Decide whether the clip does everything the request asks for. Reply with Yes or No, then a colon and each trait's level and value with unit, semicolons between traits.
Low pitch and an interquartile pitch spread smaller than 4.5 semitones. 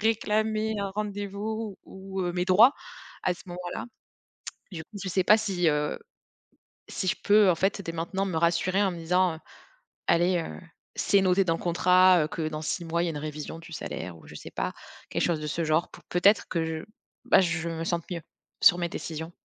No: medium, 175 Hz; average, 2.9 semitones